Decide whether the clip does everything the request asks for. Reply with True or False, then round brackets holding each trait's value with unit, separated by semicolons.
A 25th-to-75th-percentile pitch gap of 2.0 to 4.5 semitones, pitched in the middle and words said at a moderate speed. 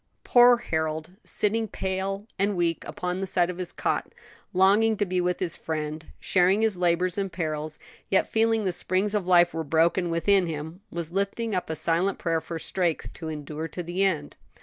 True (3.1 semitones; 180 Hz; 195 wpm)